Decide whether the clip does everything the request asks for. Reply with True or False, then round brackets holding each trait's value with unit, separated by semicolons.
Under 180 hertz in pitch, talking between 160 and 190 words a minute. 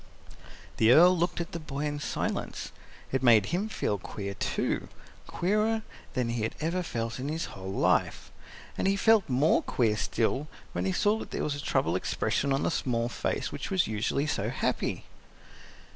True (140 Hz; 180 wpm)